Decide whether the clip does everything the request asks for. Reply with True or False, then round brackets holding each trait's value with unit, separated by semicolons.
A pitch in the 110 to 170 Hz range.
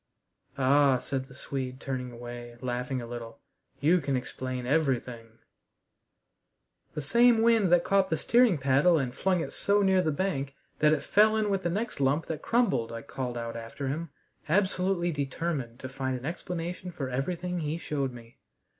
True (140 Hz)